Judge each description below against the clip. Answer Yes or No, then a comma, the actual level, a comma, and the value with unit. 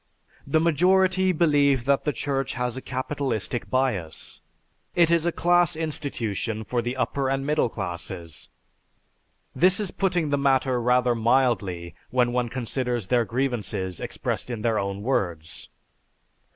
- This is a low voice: Yes, low, 130 Hz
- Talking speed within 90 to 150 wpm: Yes, average, 140 wpm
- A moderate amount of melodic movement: Yes, average, 4.5 semitones